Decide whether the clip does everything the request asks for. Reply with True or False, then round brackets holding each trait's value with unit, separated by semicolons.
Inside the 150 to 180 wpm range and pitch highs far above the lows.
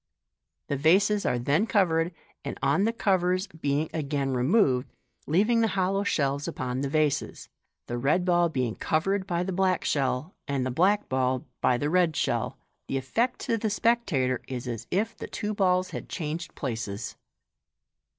True (165 wpm; 6.4 semitones)